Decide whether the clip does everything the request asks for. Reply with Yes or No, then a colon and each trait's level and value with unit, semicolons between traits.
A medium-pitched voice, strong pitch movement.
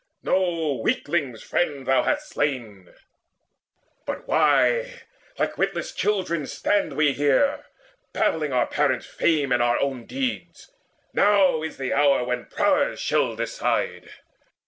Yes: medium, 150 Hz; wide, 6.5 semitones